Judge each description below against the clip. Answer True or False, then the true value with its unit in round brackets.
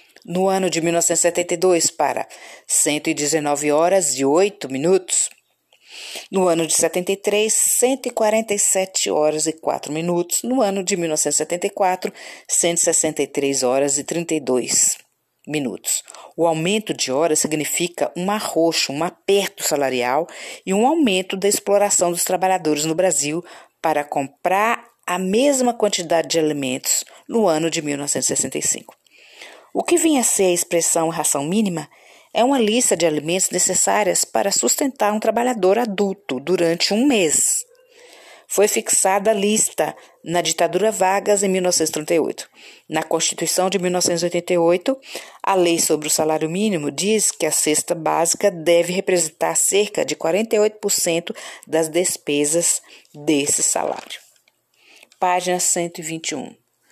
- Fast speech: False (120 wpm)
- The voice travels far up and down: False (4.0 semitones)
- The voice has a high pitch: False (175 Hz)